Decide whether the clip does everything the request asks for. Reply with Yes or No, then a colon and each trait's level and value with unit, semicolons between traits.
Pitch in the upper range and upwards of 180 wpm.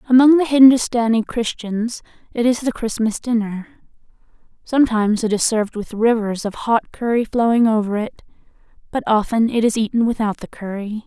No: high, 225 Hz; average, 155 wpm